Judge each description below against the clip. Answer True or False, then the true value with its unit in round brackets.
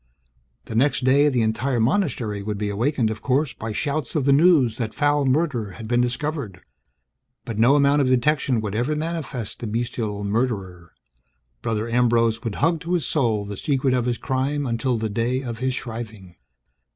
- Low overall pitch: True (120 Hz)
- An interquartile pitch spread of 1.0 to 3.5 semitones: False (4.0 semitones)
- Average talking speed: True (180 wpm)